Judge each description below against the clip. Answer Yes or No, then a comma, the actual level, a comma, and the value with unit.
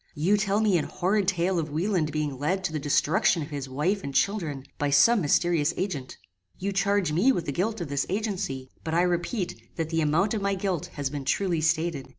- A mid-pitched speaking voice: Yes, medium, 170 Hz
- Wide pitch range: No, average, 4.8 semitones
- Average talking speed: No, fast, 215 wpm